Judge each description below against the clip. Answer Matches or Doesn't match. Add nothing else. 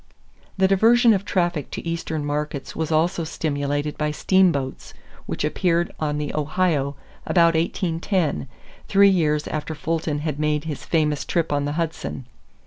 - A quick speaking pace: Doesn't match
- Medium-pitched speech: Matches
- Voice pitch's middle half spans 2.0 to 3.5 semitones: Matches